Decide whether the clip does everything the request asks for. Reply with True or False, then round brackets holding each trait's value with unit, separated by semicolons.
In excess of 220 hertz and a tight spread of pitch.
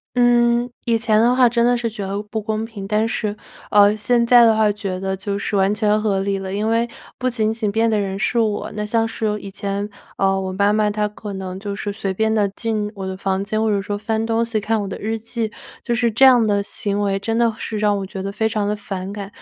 False (210 Hz; 2.0 semitones)